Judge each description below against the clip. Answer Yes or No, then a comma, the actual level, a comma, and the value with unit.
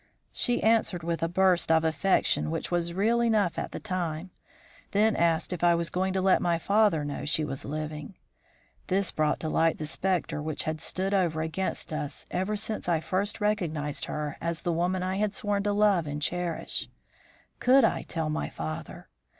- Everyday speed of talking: Yes, average, 190 wpm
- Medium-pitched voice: Yes, medium, 175 Hz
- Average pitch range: Yes, average, 3.7 semitones